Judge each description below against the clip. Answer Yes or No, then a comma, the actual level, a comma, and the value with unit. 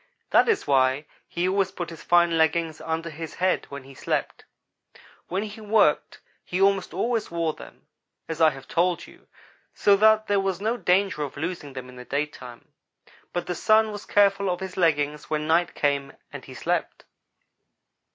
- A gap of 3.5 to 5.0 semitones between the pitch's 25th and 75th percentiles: Yes, average, 4.6 semitones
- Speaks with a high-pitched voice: No, medium, 170 Hz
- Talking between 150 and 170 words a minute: No, average, 180 wpm